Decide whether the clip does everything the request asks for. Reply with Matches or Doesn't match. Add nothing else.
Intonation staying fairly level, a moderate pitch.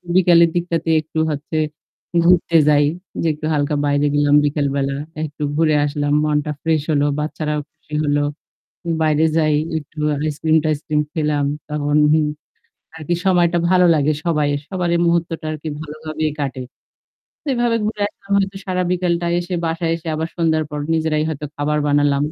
Matches